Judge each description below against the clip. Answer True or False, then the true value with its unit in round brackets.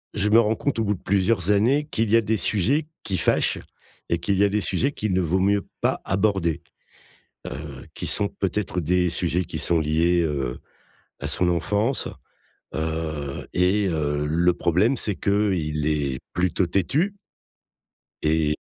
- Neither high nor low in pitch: False (90 Hz)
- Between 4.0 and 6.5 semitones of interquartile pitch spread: True (4.5 semitones)